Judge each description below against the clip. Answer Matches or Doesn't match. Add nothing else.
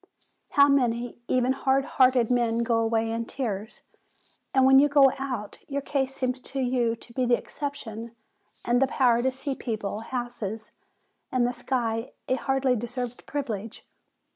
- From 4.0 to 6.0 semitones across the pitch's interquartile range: Doesn't match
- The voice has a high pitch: Matches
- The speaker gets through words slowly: Doesn't match